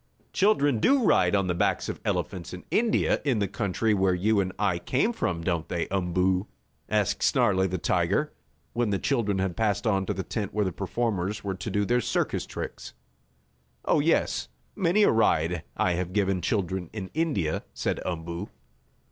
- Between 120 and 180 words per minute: Yes, average, 175 wpm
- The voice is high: No, very low, 95 Hz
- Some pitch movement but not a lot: Yes, average, 3.5 semitones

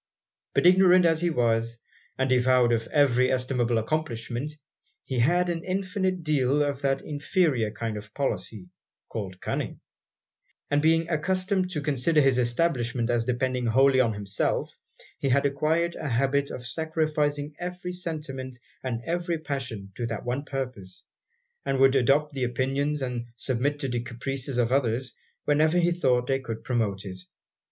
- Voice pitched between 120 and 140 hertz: Yes, low, 135 Hz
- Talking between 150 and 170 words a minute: Yes, average, 155 wpm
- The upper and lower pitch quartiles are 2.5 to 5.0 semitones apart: Yes, average, 4.3 semitones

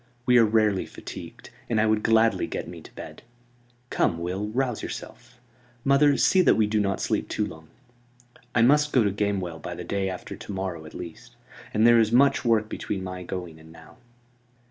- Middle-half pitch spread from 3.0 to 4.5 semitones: Yes, average, 4.2 semitones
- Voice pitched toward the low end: Yes, low, 105 Hz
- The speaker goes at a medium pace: Yes, average, 195 wpm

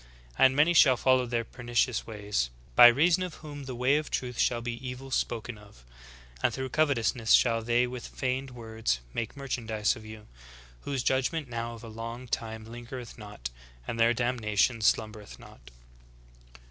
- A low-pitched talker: Yes, low, 120 Hz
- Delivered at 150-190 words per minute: Yes, average, 165 wpm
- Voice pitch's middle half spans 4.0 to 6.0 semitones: No, narrow, 2.6 semitones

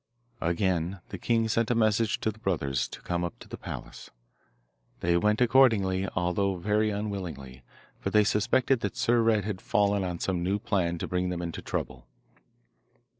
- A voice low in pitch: Yes, low, 100 Hz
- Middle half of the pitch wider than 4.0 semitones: No, average, 3.7 semitones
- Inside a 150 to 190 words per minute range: Yes, average, 175 wpm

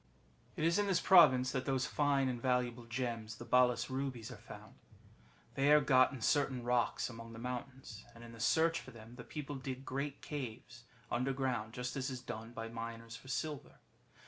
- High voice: No, low, 125 Hz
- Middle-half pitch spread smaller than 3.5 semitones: Yes, narrow, 2.6 semitones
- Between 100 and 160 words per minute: No, average, 195 wpm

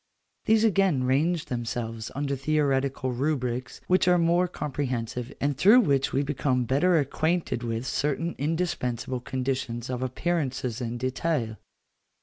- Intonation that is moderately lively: Yes, average, 4.6 semitones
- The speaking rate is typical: No, slow, 130 wpm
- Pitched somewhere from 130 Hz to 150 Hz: Yes, low, 135 Hz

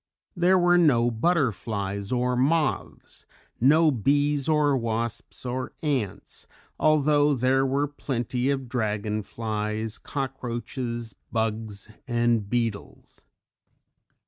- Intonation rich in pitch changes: No, average, 4.3 semitones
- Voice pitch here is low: Yes, low, 125 Hz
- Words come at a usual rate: No, slow, 90 wpm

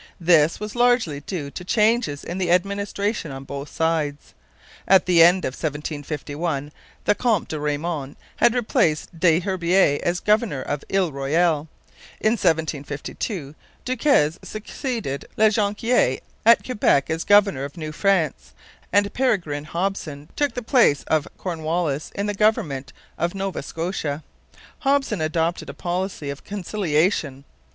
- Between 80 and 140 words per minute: Yes, slow, 135 wpm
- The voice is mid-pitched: Yes, medium, 170 Hz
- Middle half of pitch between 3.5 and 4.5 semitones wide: No, wide, 5.5 semitones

